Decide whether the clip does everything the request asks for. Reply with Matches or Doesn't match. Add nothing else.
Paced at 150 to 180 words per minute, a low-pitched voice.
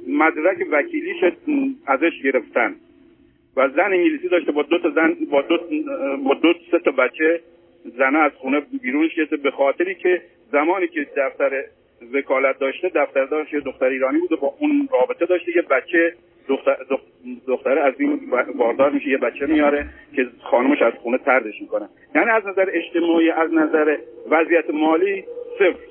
Doesn't match